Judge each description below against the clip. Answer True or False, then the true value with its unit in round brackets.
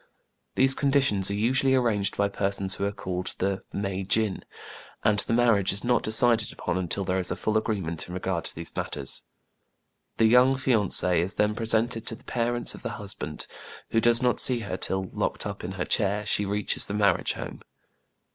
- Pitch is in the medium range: False (105 Hz)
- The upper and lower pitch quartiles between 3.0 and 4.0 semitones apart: True (3.4 semitones)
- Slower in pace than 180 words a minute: False (195 wpm)